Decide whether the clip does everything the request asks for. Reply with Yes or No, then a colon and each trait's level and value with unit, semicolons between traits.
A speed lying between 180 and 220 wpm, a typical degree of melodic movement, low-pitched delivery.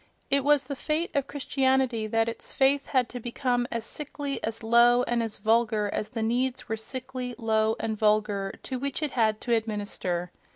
No: average, 190 wpm; average, 3.2 semitones; high, 235 Hz